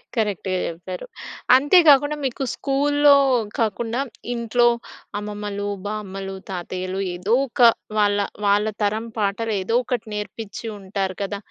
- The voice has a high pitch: Yes, high, 210 Hz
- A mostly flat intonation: No, average, 3.4 semitones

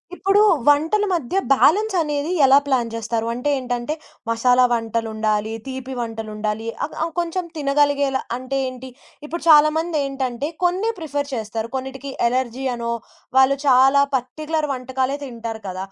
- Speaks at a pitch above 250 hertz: Yes, very high, 265 Hz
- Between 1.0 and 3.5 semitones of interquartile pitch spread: No, average, 4.0 semitones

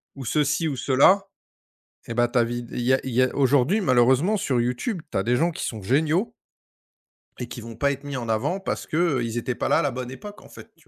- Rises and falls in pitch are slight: No, average, 4.4 semitones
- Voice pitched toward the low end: Yes, low, 130 Hz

